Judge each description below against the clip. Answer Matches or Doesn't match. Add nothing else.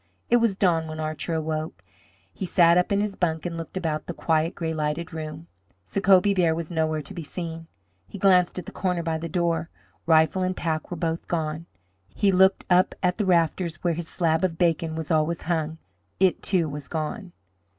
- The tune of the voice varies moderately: Doesn't match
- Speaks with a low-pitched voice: Doesn't match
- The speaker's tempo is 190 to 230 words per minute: Matches